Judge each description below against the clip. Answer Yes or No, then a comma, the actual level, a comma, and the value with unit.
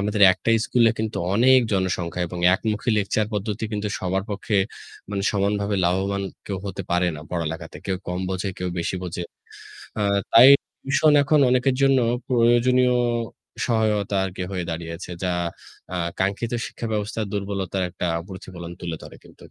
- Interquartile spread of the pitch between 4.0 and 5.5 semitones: No, average, 3.6 semitones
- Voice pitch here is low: Yes, low, 100 Hz